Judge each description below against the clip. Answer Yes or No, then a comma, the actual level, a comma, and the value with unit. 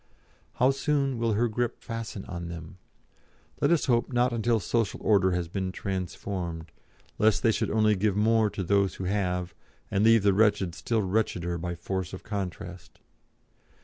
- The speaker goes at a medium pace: Yes, average, 165 wpm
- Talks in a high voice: No, low, 100 Hz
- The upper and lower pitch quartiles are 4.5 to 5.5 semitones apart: No, average, 3.8 semitones